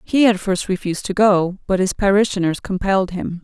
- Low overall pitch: No, high, 190 Hz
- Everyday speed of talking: Yes, average, 190 wpm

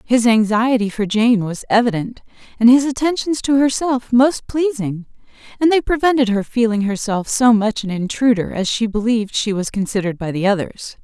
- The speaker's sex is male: No, female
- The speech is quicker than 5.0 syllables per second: Yes, 5.2 syllables/s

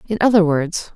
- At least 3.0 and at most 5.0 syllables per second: No, 5.3 syllables/s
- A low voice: No, medium, 185 Hz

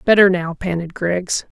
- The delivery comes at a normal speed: Yes, average, 150 wpm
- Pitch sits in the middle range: Yes, medium, 180 Hz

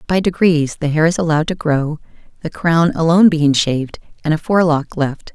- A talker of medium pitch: Yes, medium, 160 Hz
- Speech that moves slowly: No, average, 190 wpm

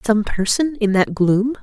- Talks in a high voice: Yes, high, 220 Hz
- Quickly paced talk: No, average, 185 wpm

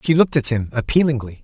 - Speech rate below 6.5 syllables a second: No, 6.9 syllables/s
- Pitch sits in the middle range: No, low, 130 Hz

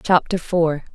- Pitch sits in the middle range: Yes, medium, 170 Hz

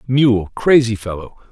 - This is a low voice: Yes, low, 115 Hz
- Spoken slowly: Yes, slow, 120 wpm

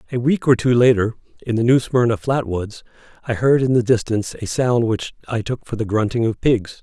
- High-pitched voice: No, low, 120 Hz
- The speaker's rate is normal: No, fast, 230 wpm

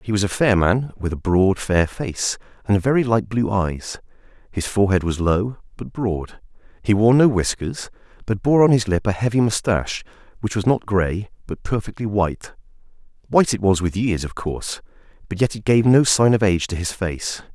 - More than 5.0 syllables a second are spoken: Yes, 5.2 syllables/s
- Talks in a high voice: No, low, 105 Hz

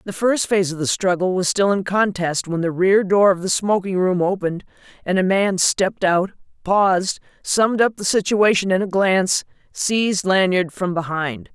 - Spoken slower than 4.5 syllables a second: No, 5.0 syllables/s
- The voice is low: No, high, 190 Hz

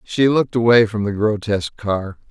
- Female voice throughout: No, male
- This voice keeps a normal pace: Yes, average, 180 wpm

